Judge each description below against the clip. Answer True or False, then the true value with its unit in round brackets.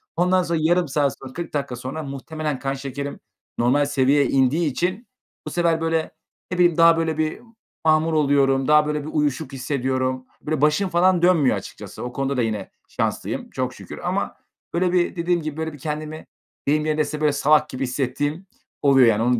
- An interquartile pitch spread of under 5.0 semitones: True (3.2 semitones)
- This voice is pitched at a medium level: True (150 Hz)